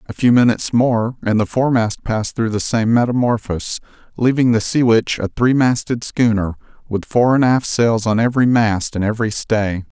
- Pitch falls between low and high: No, low, 115 Hz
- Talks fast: No, average, 185 wpm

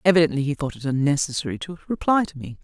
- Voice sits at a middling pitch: Yes, medium, 155 Hz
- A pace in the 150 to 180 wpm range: No, fast, 205 wpm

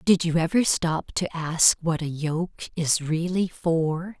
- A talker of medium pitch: Yes, medium, 165 Hz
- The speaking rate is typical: Yes, average, 170 wpm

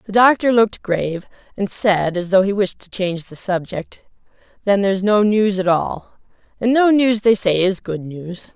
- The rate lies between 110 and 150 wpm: No, average, 195 wpm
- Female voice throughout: Yes, female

